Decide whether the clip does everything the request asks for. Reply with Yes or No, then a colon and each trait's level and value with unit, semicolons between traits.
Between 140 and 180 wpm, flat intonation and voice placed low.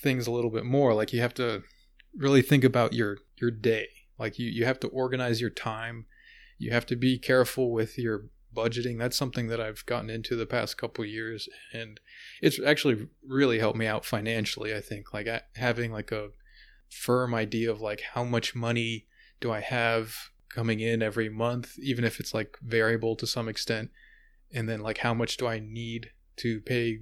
No: average, 200 wpm; narrow, 1.6 semitones; low, 115 Hz